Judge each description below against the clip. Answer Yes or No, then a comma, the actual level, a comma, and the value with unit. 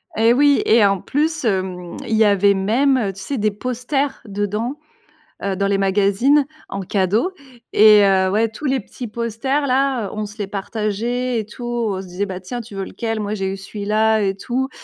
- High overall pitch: Yes, high, 215 Hz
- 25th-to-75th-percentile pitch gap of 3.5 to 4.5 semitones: Yes, average, 3.9 semitones